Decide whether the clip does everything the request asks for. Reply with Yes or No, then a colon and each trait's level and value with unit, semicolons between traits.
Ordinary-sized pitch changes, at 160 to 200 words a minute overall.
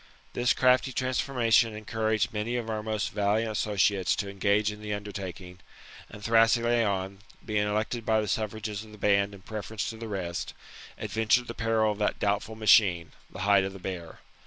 No: narrow, 1.9 semitones; average, 175 wpm